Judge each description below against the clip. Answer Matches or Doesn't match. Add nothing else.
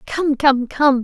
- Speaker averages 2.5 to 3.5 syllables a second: Matches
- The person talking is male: Doesn't match